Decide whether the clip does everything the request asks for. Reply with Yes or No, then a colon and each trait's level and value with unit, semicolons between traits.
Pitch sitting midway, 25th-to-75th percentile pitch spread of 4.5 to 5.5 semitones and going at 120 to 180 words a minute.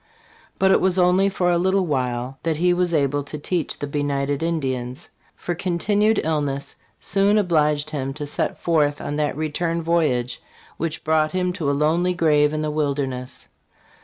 No: medium, 155 Hz; average, 3.6 semitones; average, 170 wpm